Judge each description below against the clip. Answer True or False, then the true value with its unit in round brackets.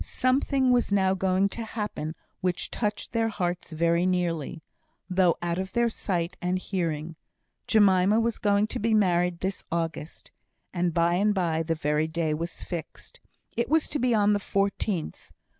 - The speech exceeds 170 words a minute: False (165 wpm)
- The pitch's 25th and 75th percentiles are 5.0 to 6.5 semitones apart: False (3.7 semitones)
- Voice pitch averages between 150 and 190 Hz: True (185 Hz)